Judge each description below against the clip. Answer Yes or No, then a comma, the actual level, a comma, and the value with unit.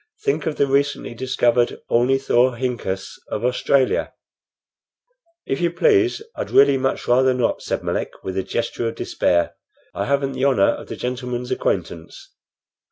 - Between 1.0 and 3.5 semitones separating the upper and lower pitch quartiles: Yes, narrow, 2.5 semitones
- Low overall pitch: Yes, low, 130 Hz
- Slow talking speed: No, average, 145 wpm